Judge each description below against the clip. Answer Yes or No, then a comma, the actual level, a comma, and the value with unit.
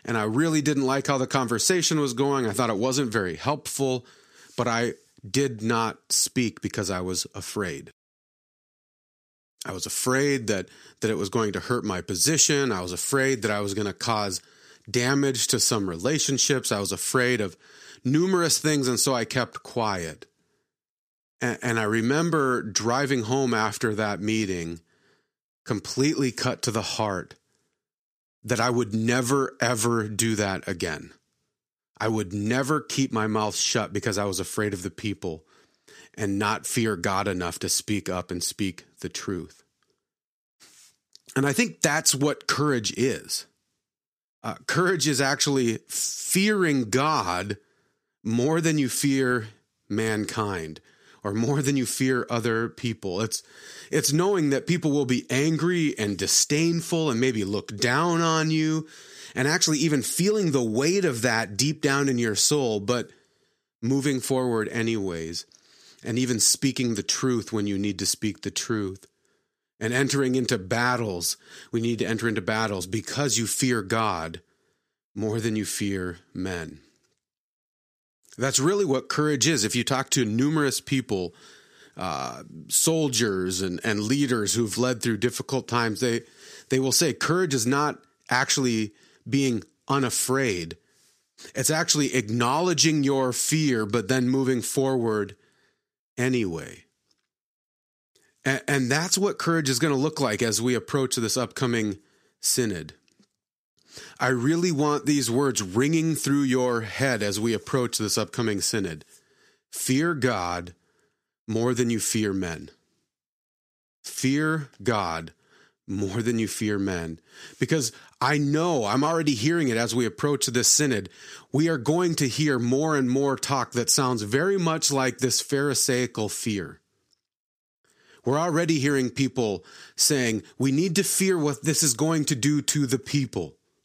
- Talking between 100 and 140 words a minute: No, average, 150 wpm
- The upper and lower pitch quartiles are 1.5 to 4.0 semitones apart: No, average, 4.6 semitones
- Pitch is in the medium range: No, low, 125 Hz